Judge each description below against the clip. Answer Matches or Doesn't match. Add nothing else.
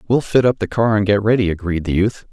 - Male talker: Matches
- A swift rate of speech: Matches